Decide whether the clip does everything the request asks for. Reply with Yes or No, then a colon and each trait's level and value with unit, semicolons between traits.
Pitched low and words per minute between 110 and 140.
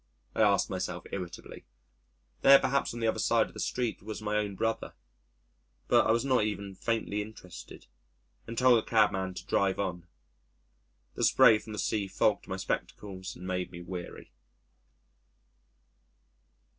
No: low, 105 Hz; average, 155 wpm